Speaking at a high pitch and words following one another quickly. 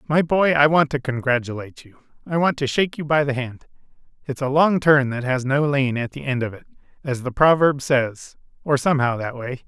No: medium, 140 Hz; fast, 225 wpm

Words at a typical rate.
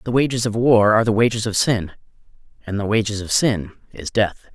No: fast, 210 wpm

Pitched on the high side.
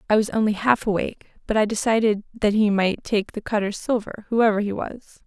Yes: high, 215 Hz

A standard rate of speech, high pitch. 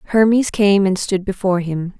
Yes: average, 180 wpm; high, 195 Hz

